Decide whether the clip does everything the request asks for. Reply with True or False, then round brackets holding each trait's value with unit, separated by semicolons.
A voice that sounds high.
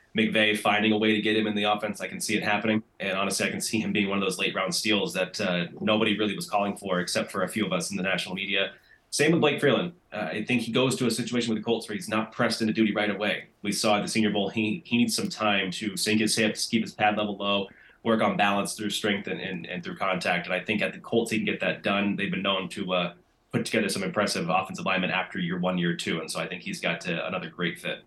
False (105 Hz)